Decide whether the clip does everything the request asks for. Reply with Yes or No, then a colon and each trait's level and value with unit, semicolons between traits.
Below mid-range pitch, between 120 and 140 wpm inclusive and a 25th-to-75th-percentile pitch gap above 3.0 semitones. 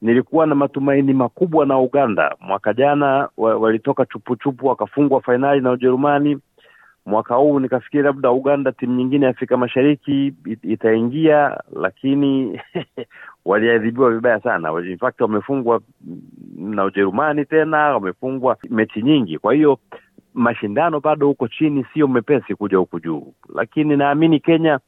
Yes: low, 130 Hz; average, 130 wpm; average, 3.7 semitones